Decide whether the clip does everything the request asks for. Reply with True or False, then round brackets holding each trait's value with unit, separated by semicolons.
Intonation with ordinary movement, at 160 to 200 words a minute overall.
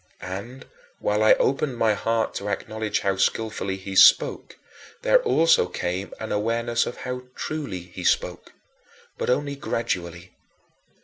False (4.6 semitones; 135 wpm)